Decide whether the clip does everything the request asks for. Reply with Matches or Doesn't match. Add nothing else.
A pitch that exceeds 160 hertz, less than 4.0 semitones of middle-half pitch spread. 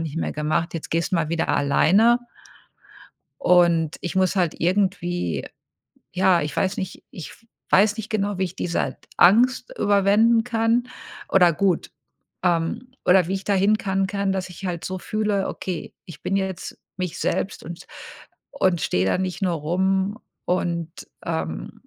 Matches